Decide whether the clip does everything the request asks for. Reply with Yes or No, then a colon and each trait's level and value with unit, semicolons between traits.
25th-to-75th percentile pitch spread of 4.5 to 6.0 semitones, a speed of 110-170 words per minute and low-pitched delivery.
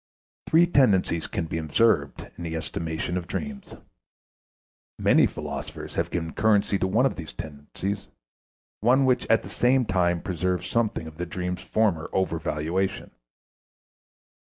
Yes: average, 5.3 semitones; average, 140 wpm; very low, 90 Hz